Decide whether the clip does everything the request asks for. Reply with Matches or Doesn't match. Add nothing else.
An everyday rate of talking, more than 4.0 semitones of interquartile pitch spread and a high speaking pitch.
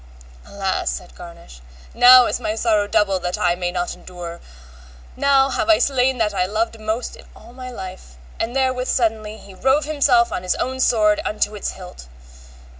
Matches